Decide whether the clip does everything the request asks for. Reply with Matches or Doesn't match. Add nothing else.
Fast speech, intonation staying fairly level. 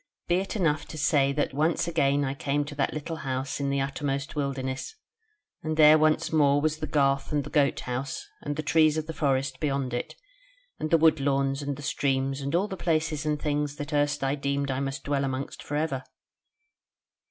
Matches